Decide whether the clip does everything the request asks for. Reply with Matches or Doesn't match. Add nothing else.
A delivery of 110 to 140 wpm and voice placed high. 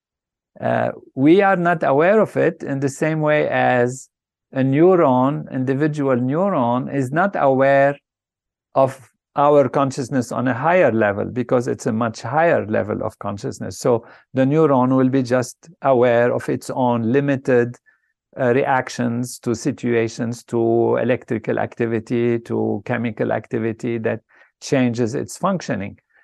Doesn't match